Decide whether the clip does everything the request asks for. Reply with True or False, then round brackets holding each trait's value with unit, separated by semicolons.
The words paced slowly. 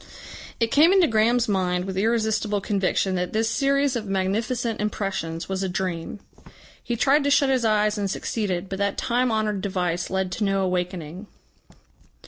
False (165 wpm)